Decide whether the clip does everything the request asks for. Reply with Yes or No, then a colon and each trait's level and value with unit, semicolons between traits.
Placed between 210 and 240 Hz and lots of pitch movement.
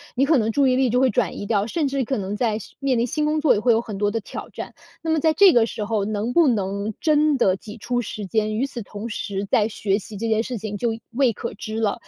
No: high, 225 Hz; average, 4.2 semitones